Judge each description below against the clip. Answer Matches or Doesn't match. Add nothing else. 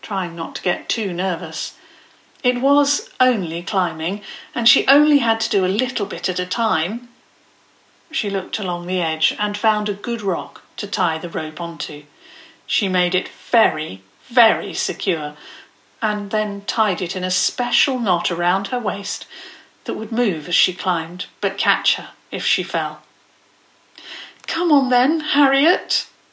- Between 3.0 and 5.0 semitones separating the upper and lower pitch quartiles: Doesn't match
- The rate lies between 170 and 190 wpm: Doesn't match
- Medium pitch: Doesn't match